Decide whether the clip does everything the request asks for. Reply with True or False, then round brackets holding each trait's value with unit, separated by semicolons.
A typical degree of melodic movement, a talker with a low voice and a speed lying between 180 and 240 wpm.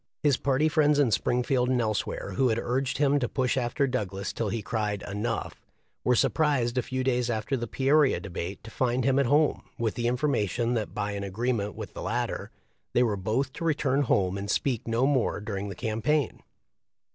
True (3.9 semitones; 120 Hz; 200 wpm)